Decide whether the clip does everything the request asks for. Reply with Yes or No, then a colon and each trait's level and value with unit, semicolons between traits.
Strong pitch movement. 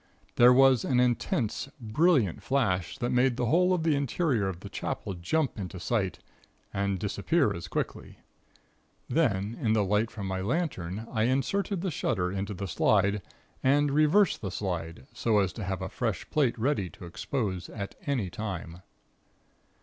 Yes: wide, 6.0 semitones